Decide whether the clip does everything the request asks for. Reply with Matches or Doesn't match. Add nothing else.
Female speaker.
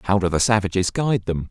Doesn't match